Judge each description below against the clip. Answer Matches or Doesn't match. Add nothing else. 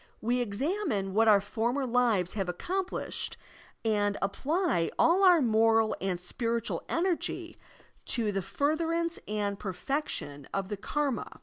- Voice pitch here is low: Doesn't match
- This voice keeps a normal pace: Doesn't match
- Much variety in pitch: Matches